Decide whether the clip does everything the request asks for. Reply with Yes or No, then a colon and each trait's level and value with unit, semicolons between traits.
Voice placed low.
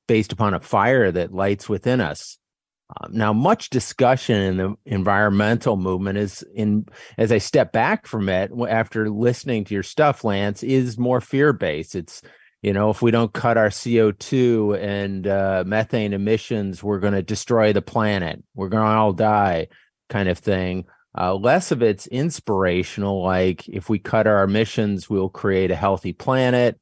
Yes: low, 105 Hz